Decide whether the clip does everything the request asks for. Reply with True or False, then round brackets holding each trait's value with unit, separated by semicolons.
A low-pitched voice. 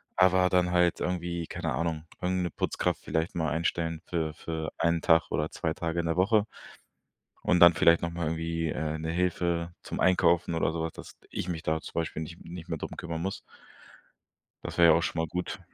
True (85 Hz)